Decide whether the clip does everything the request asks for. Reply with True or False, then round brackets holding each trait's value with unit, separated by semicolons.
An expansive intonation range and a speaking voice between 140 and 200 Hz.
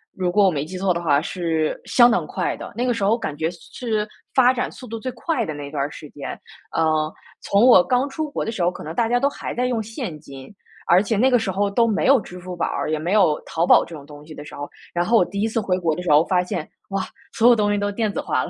True (6.0 semitones; 195 Hz)